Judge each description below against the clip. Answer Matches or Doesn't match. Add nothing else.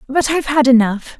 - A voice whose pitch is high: Matches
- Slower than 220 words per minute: Matches